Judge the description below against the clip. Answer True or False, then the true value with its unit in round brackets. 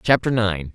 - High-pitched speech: False (110 Hz)